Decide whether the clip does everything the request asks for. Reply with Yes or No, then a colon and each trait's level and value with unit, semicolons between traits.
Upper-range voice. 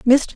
Yes: very high, 260 Hz